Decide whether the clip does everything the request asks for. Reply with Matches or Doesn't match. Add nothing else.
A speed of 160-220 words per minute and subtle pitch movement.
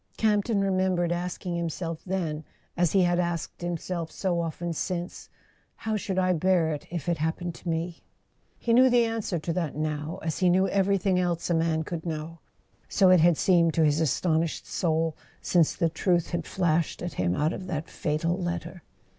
Matches